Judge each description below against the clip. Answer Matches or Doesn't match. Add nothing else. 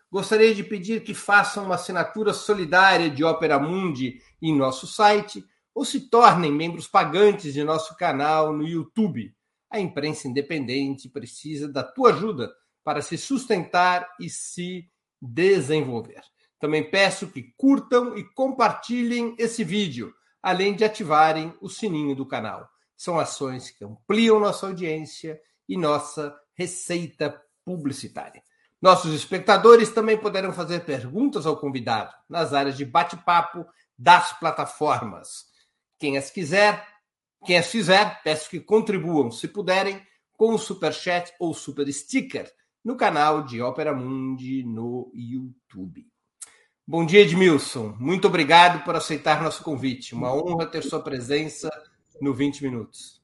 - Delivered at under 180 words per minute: Matches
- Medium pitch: Matches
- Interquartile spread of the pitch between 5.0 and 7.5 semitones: Matches